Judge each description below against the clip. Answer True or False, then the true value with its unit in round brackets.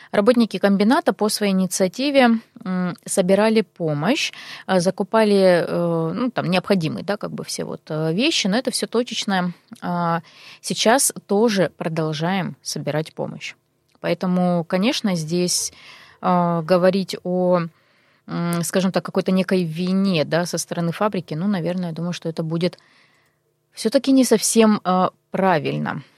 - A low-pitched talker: False (185 Hz)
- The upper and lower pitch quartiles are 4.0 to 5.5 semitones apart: False (3.5 semitones)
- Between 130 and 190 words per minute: False (115 wpm)